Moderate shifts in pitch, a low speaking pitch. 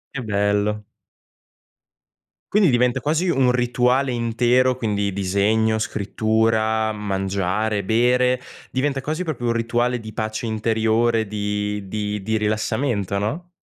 Yes: average, 3.1 semitones; low, 110 Hz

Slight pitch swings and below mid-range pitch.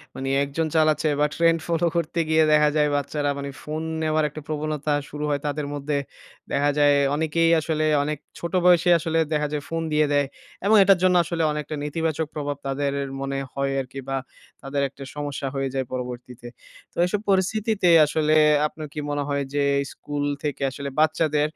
No: narrow, 2.1 semitones; medium, 150 Hz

